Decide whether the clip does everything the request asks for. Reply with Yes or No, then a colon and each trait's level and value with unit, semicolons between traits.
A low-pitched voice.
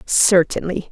No: medium, 180 Hz